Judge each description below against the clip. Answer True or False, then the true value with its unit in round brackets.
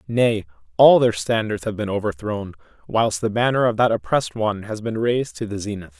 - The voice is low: True (115 Hz)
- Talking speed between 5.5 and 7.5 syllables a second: True (5.8 syllables/s)